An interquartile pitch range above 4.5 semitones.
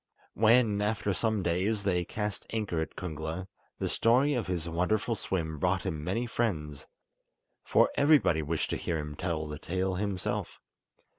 Yes: average, 4.9 semitones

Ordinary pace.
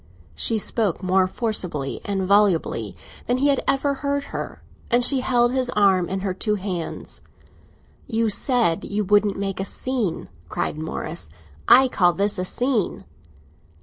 Yes: average, 150 wpm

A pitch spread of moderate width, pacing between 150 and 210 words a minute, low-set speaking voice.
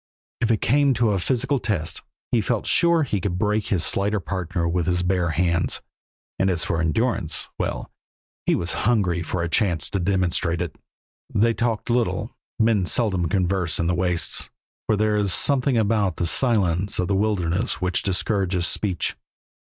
Yes: average, 4.1 semitones; average, 170 wpm; very low, 95 Hz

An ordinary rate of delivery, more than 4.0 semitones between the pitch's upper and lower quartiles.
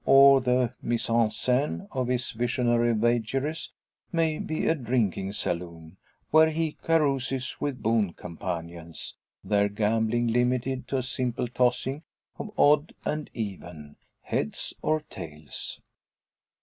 No: slow, 125 wpm; average, 4.5 semitones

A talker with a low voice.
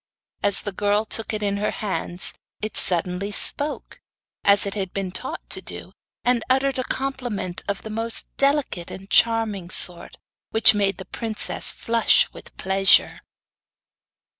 No: high, 205 Hz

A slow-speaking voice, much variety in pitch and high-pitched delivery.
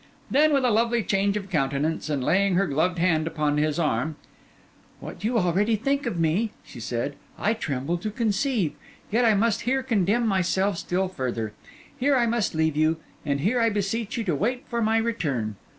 No: average, 190 wpm; wide, 6.5 semitones; high, 195 Hz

